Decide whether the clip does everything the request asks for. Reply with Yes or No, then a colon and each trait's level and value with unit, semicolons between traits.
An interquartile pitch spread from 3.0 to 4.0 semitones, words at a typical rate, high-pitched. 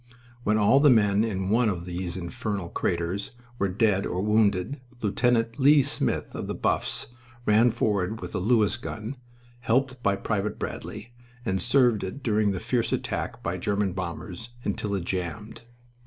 No: average, 3.5 semitones; average, 160 wpm; low, 105 Hz